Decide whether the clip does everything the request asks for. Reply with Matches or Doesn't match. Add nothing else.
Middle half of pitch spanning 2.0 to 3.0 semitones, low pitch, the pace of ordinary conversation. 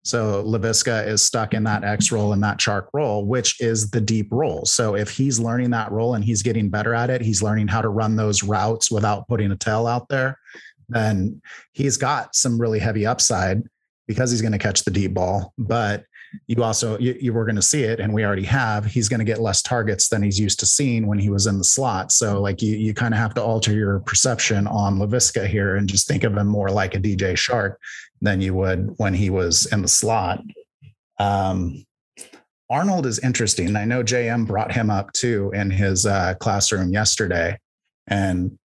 Doesn't match